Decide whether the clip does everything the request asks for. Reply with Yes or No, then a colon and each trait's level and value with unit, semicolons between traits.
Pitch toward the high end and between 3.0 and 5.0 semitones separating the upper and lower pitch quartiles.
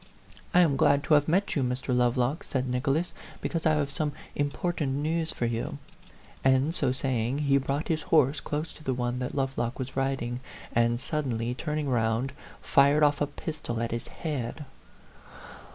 No: low, 135 Hz; average, 3.3 semitones